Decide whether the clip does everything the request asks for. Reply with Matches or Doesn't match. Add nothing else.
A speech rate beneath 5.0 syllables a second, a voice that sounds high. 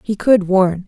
Matches